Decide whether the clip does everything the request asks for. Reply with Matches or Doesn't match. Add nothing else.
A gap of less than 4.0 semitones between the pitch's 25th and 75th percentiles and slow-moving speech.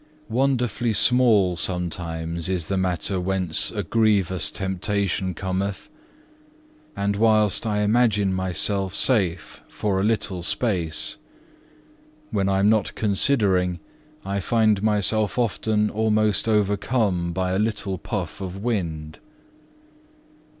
Matches